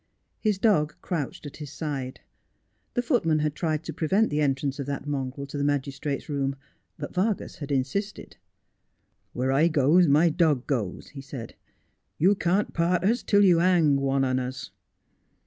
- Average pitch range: Yes, average, 4.2 semitones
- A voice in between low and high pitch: Yes, medium, 150 Hz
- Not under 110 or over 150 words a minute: No, average, 175 wpm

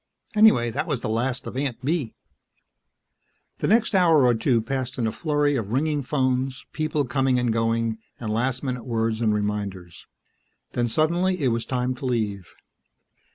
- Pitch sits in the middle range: No, low, 125 Hz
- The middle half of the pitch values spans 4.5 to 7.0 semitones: No, average, 4.1 semitones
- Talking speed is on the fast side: No, average, 165 wpm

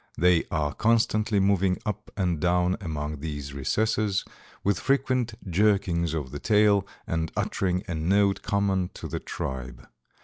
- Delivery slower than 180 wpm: Yes, average, 140 wpm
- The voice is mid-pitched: No, very low, 90 Hz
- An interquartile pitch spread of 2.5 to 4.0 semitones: No, average, 4.4 semitones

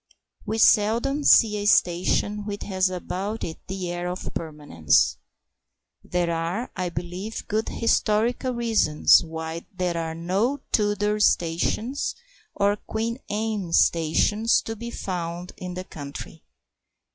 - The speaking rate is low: Yes, slow, 125 wpm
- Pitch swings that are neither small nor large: Yes, average, 4.4 semitones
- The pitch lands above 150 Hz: Yes, high, 190 Hz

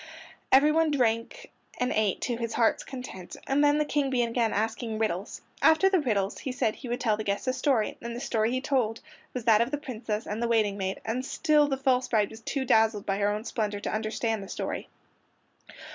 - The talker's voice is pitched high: Yes, high, 230 Hz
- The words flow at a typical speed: No, fast, 215 wpm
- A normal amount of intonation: Yes, average, 3.4 semitones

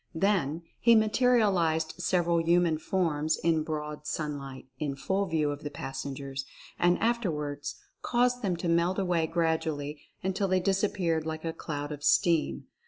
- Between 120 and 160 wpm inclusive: Yes, average, 150 wpm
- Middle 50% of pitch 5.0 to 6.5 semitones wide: No, average, 3.8 semitones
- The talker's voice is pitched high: No, medium, 165 Hz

